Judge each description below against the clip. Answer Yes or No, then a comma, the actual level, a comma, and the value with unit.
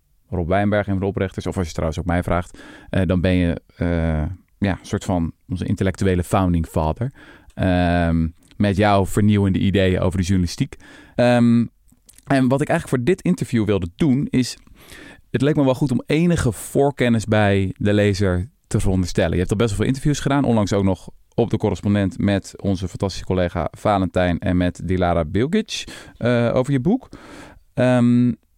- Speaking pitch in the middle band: No, low, 100 Hz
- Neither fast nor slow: Yes, average, 175 wpm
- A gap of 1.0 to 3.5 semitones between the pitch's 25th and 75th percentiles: No, average, 5.0 semitones